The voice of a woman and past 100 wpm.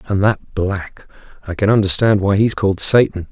No: male; average, 200 wpm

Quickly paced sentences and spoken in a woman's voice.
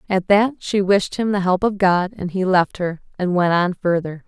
Yes: fast, 240 wpm; female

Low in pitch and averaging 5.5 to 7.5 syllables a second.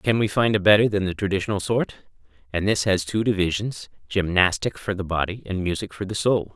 Yes: low, 100 Hz; 5.8 syllables/s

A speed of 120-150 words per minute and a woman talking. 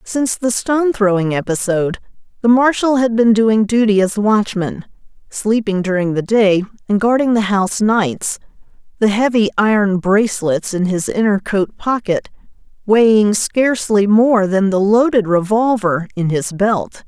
Yes: average, 145 wpm; female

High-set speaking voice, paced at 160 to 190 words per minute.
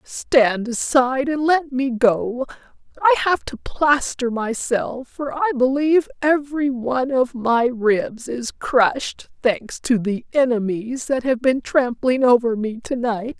No: very high, 255 Hz; average, 150 wpm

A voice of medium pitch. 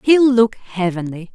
No: high, 215 Hz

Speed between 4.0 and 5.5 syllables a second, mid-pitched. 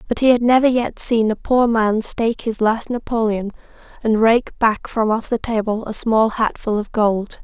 No: 4.6 syllables/s; high, 225 Hz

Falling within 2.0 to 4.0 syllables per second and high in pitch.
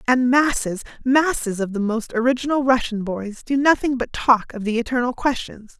No: 5.1 syllables/s; high, 245 Hz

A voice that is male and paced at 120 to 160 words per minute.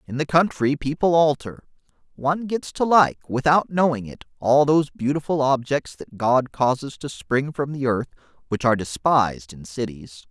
No: male; average, 170 wpm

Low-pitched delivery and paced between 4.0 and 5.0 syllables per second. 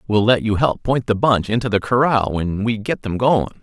No: low, 110 Hz; 5.2 syllables/s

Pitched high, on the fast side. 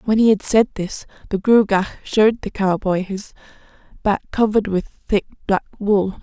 No: high, 205 Hz; average, 165 wpm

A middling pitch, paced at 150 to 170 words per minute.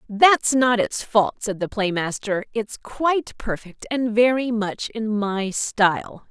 No: high, 220 Hz; average, 160 wpm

